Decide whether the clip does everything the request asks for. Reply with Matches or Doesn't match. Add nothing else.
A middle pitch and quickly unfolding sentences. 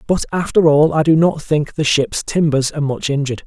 Matches